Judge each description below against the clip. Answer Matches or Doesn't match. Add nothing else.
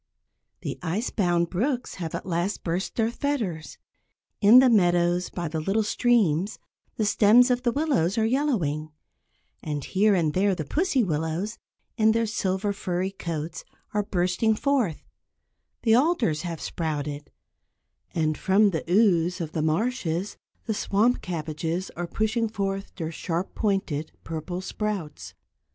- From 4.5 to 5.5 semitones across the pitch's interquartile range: Matches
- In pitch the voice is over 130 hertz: Matches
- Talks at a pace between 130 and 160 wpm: Matches